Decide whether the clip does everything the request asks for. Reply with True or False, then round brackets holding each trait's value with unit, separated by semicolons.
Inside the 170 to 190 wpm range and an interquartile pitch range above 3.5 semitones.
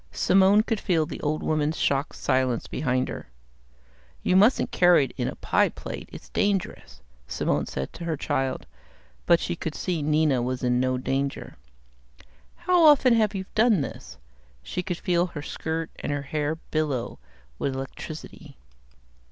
False (160 wpm; 5.3 semitones)